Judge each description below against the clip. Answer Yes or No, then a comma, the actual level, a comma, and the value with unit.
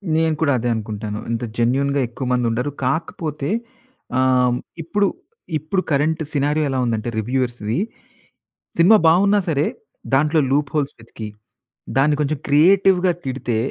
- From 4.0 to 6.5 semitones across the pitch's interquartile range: Yes, average, 4.4 semitones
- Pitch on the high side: No, medium, 140 Hz